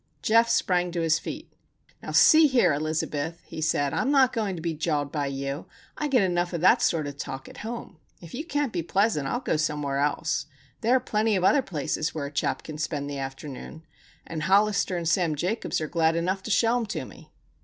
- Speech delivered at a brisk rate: Yes, fast, 220 wpm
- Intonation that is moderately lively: No, wide, 6.3 semitones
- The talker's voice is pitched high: No, medium, 170 Hz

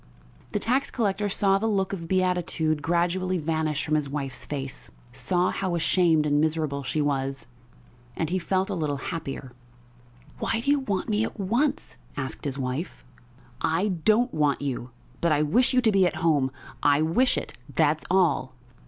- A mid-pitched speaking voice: Yes, medium, 165 Hz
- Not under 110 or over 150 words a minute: No, average, 170 wpm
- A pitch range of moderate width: Yes, average, 4.8 semitones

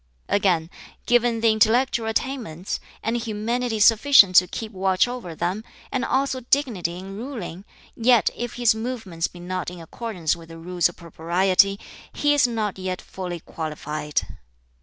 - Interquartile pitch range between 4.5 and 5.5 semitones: Yes, average, 5.2 semitones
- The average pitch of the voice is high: Yes, high, 205 Hz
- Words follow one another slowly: No, average, 150 wpm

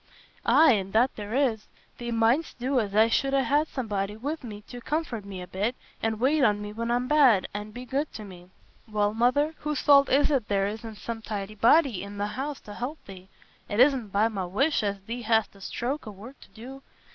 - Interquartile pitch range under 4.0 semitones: No, average, 4.5 semitones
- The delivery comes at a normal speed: No, fast, 220 wpm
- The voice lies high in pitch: Yes, high, 225 Hz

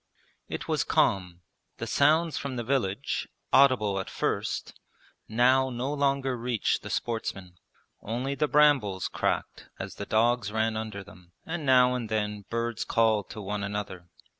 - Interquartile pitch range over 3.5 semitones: Yes, average, 4.4 semitones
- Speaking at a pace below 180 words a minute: Yes, average, 150 wpm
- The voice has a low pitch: Yes, low, 115 Hz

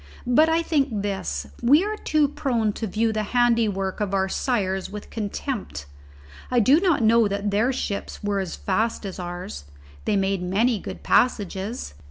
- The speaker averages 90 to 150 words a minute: No, average, 175 wpm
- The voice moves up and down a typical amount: Yes, average, 4.1 semitones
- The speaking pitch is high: Yes, high, 210 Hz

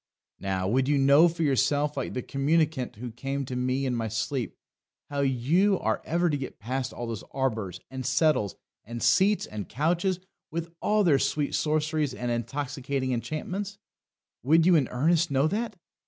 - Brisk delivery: No, average, 170 wpm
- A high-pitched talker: No, medium, 140 Hz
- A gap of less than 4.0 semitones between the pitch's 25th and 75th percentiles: No, average, 4.4 semitones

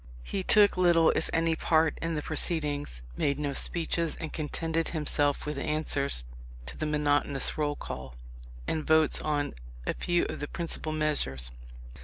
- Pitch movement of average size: No, narrow, 2.1 semitones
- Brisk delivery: No, average, 155 wpm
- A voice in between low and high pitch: Yes, medium, 155 Hz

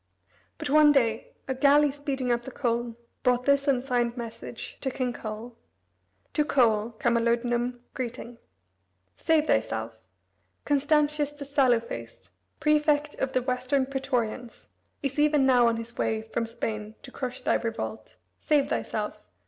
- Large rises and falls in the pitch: No, average, 3.2 semitones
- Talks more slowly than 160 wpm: Yes, average, 140 wpm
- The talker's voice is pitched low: No, very high, 250 Hz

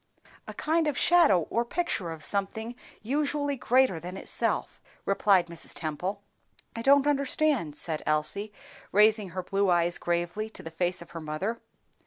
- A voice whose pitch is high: Yes, high, 200 Hz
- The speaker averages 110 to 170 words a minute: Yes, average, 155 wpm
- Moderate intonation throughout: No, wide, 6.9 semitones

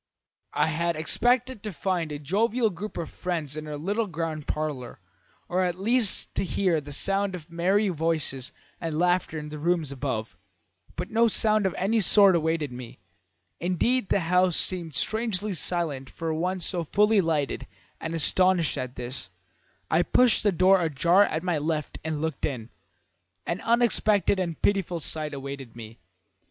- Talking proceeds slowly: No, average, 165 wpm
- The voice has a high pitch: No, medium, 170 Hz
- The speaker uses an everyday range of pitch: Yes, average, 4.3 semitones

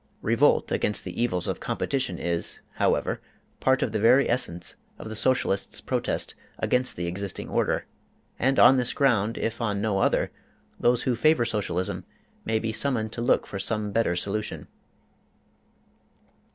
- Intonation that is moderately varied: Yes, average, 3.8 semitones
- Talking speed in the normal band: Yes, average, 150 wpm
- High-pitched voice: No, low, 110 Hz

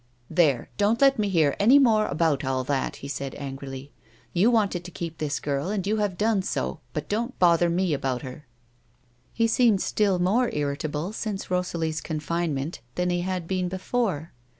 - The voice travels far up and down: Yes, wide, 5.9 semitones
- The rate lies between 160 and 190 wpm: Yes, average, 180 wpm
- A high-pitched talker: No, medium, 175 Hz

